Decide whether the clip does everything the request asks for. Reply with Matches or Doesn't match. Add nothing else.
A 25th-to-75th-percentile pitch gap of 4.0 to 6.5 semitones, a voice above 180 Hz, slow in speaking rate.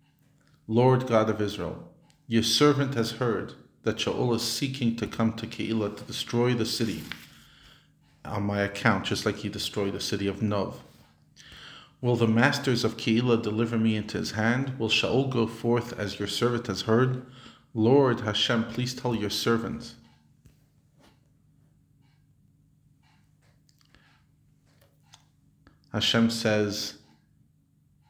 Doesn't match